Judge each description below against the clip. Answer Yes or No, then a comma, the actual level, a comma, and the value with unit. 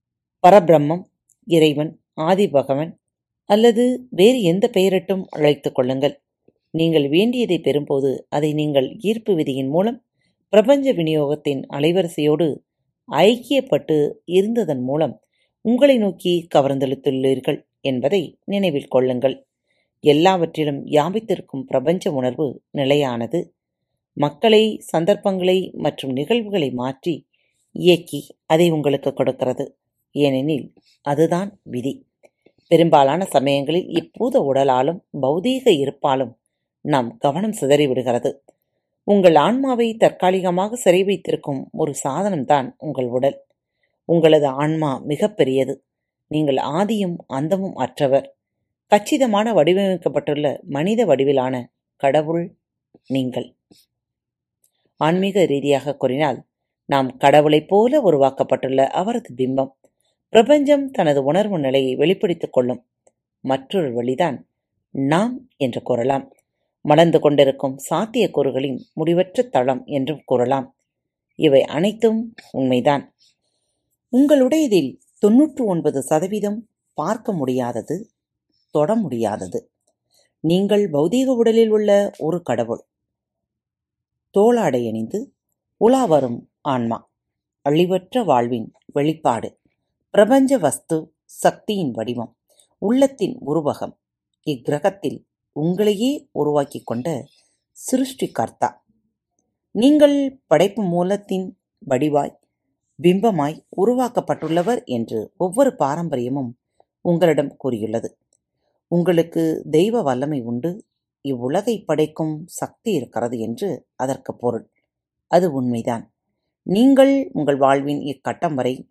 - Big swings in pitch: Yes, wide, 6.7 semitones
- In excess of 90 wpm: No, average, 85 wpm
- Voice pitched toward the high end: No, medium, 155 Hz